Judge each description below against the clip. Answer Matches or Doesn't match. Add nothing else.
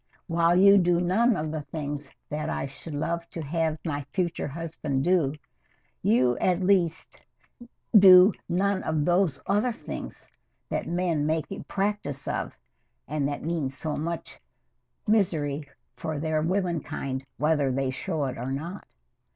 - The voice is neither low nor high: Matches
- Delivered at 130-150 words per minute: Matches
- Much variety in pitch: Doesn't match